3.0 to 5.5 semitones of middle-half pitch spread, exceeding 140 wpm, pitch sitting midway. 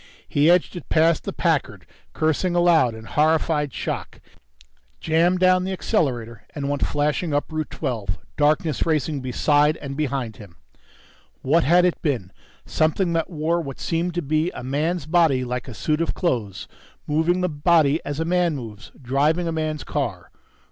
Yes: average, 3.5 semitones; average, 165 wpm; medium, 155 Hz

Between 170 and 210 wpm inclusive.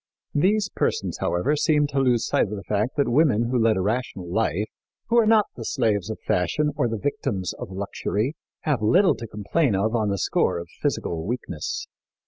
Yes: average, 195 wpm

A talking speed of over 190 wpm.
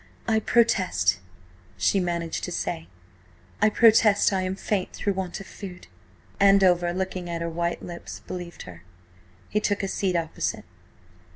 No: average, 150 wpm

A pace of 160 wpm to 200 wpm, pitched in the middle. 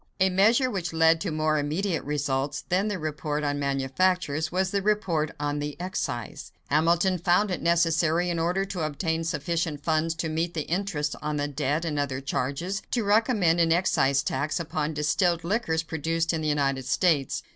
Yes: average, 180 wpm; medium, 160 Hz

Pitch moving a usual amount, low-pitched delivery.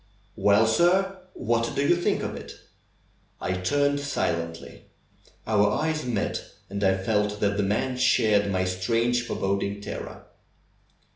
Yes: average, 4.5 semitones; low, 105 Hz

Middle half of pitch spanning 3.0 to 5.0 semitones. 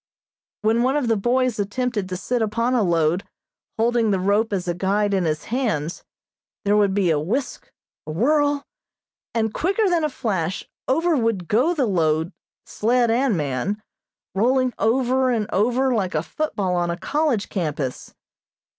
No: wide, 5.6 semitones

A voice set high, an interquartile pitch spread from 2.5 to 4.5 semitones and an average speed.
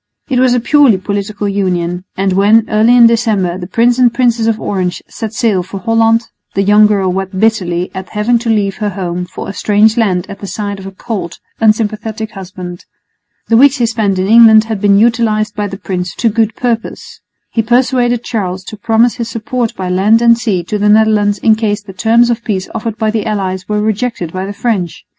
No: high, 215 Hz; average, 2.9 semitones; fast, 210 wpm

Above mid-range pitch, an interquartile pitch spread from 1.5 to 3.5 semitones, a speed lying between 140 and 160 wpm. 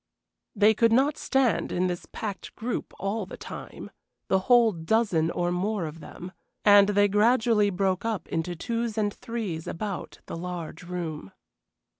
No: high, 200 Hz; average, 4.1 semitones; average, 155 wpm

